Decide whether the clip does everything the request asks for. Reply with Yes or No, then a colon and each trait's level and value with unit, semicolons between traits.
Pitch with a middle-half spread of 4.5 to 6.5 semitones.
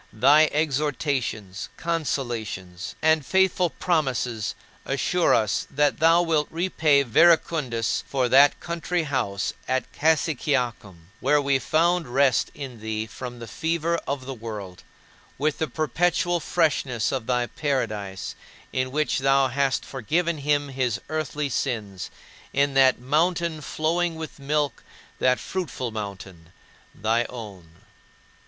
Yes: average, 5.1 semitones